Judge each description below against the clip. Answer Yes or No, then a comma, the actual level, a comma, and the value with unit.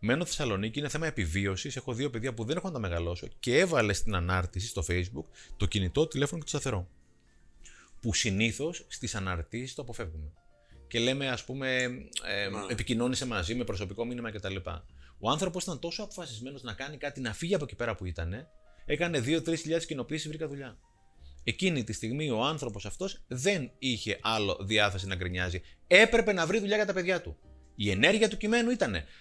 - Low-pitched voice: Yes, low, 120 Hz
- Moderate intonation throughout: No, wide, 7.6 semitones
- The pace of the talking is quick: Yes, fast, 185 wpm